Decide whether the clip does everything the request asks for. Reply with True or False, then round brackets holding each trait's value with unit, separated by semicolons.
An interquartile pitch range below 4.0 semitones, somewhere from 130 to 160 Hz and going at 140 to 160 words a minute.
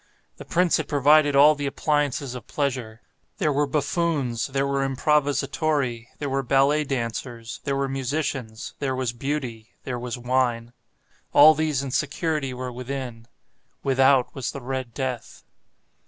True (2.7 semitones; 135 Hz; 145 wpm)